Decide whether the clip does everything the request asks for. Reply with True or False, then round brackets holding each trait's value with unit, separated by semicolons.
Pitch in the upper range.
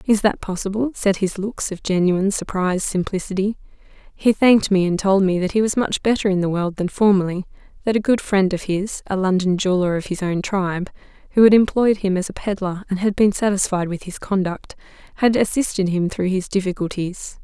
True (195 Hz)